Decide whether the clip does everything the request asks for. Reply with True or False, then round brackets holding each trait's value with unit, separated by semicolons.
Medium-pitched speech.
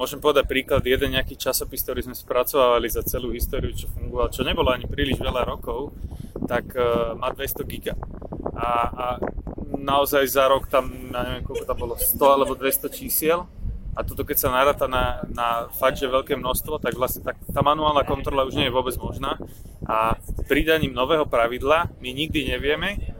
False (130 Hz)